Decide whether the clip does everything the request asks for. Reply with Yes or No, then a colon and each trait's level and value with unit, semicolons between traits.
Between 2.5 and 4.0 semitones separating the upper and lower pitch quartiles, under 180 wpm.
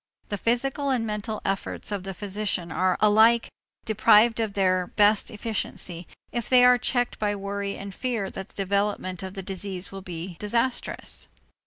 Yes: average, 2.9 semitones; average, 165 wpm